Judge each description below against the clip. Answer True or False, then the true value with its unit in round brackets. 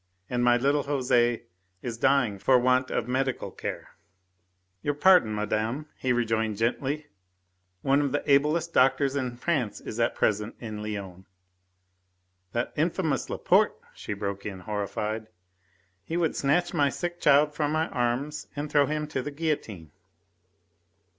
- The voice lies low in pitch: True (130 Hz)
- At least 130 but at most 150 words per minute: True (145 wpm)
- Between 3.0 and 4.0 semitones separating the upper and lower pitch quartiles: False (5.3 semitones)